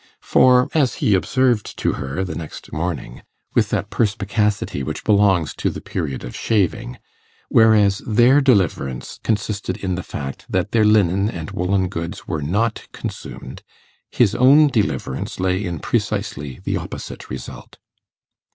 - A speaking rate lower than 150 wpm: Yes, average, 140 wpm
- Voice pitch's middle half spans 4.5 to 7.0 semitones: Yes, average, 5.2 semitones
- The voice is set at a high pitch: No, low, 100 Hz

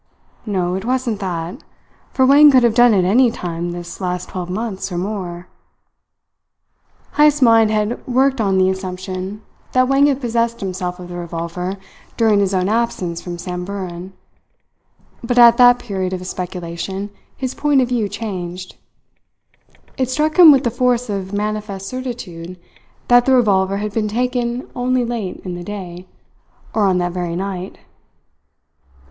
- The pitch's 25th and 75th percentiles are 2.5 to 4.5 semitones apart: No, average, 5.0 semitones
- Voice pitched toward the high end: Yes, high, 200 Hz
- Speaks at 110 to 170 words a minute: Yes, average, 160 wpm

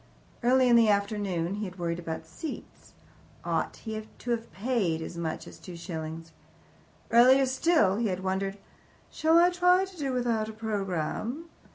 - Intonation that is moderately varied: No, wide, 6.0 semitones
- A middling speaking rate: Yes, average, 165 wpm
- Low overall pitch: No, high, 215 Hz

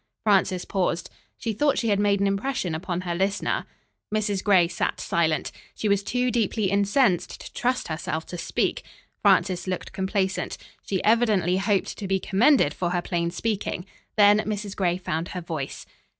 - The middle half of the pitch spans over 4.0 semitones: No, average, 2.9 semitones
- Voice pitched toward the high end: Yes, high, 195 Hz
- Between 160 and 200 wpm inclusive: Yes, average, 165 wpm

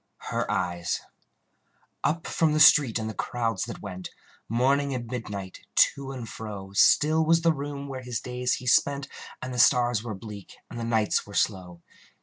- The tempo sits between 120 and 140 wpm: No, average, 175 wpm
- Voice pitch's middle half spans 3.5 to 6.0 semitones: Yes, average, 4.9 semitones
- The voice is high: No, low, 120 Hz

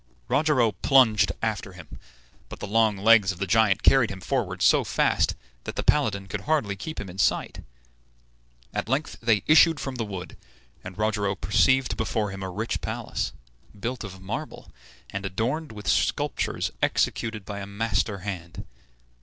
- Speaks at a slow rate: No, average, 160 wpm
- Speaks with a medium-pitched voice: No, low, 105 Hz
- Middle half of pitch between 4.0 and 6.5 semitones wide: No, average, 3.5 semitones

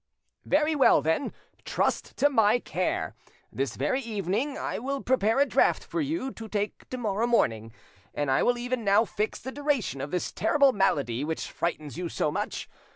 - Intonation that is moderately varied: No, wide, 7.5 semitones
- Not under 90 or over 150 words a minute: No, average, 180 wpm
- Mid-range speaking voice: No, high, 225 Hz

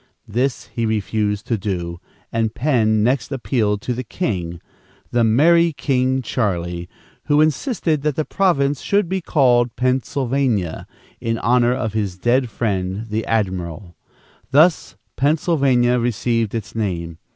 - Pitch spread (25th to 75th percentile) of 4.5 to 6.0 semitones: Yes, average, 4.8 semitones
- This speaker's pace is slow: Yes, slow, 130 wpm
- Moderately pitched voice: No, low, 120 Hz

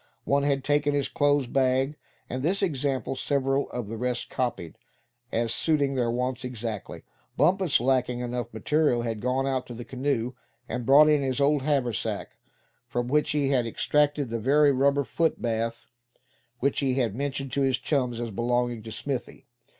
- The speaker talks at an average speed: Yes, average, 165 wpm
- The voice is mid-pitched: No, low, 130 Hz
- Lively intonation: No, average, 2.8 semitones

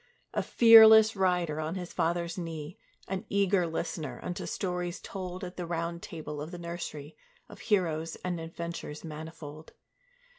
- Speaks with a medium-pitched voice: Yes, medium, 170 Hz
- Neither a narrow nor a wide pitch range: No, narrow, 2.2 semitones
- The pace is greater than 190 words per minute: No, average, 145 wpm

